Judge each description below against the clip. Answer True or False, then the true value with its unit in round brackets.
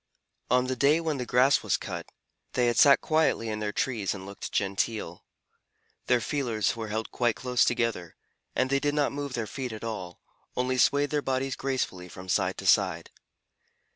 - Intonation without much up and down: False (4.1 semitones)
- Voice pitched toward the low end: True (125 Hz)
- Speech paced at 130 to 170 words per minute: False (185 wpm)